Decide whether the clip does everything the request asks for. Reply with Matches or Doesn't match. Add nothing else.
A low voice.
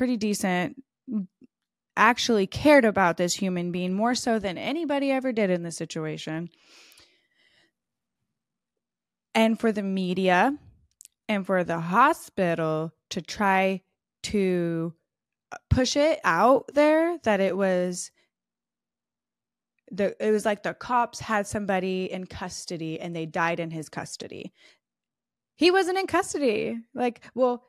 Doesn't match